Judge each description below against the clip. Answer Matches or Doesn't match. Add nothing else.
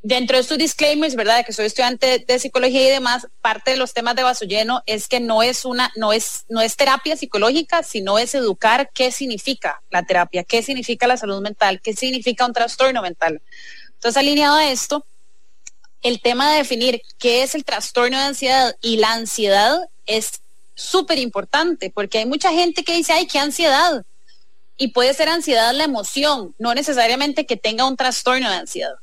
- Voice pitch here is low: Doesn't match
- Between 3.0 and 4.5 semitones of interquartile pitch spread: Matches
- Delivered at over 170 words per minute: Matches